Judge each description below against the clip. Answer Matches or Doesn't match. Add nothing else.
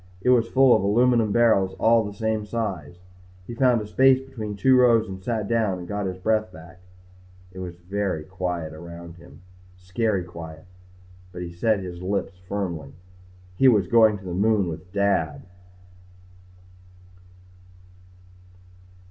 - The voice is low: Matches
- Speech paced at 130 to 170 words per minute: Matches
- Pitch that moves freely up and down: Doesn't match